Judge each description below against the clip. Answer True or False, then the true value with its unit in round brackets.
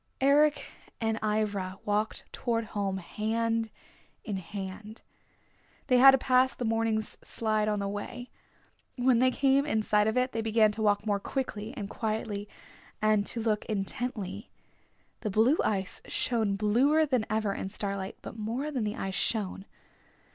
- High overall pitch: True (220 Hz)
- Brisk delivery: False (155 wpm)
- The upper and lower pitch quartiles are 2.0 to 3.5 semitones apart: True (2.9 semitones)